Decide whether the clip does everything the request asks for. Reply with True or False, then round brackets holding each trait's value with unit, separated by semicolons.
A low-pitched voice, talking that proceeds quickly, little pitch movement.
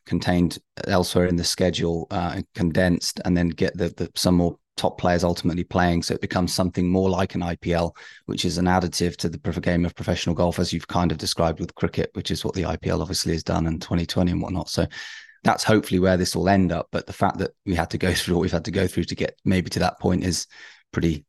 True (90 Hz; 240 wpm; 1.3 semitones)